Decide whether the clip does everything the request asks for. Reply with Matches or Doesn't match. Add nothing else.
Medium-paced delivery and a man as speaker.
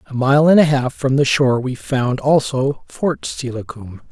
Matches